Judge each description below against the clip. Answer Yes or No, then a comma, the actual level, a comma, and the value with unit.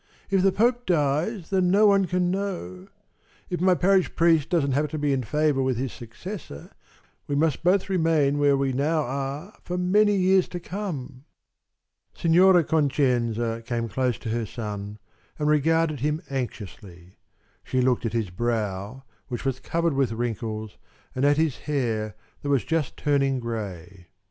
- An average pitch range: No, wide, 6.4 semitones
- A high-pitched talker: No, medium, 140 Hz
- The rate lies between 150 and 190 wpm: Yes, average, 160 wpm